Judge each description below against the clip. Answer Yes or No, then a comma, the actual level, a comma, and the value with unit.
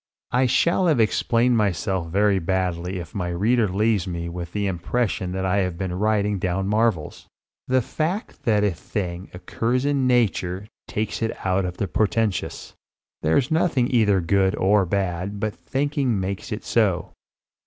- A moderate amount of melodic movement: Yes, average, 4.0 semitones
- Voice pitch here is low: Yes, low, 100 Hz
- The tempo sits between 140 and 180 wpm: Yes, average, 160 wpm